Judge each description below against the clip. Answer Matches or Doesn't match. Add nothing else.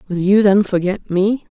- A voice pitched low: Doesn't match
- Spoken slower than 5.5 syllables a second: Matches